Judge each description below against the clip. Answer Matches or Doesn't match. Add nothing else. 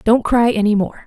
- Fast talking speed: Matches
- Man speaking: Doesn't match